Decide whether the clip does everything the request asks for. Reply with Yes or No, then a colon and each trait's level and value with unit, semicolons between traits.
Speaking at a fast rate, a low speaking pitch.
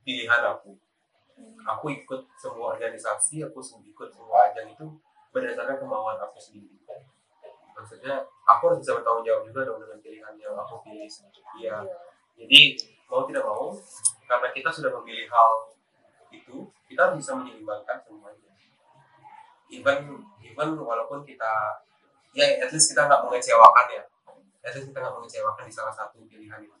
No: fast, 150 wpm; medium, 155 Hz